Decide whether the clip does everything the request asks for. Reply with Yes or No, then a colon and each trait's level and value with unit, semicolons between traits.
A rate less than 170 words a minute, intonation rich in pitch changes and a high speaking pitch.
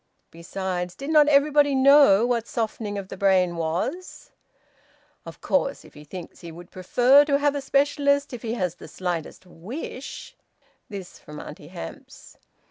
Yes: average, 160 wpm; wide, 7.8 semitones; high, 225 Hz